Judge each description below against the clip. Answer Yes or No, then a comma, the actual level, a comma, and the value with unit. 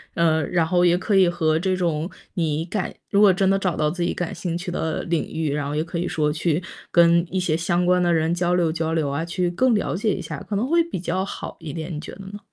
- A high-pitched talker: No, medium, 170 Hz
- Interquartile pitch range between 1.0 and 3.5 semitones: Yes, narrow, 2.4 semitones